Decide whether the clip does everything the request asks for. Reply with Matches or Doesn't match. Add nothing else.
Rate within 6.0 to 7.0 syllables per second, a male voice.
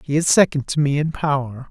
Doesn't match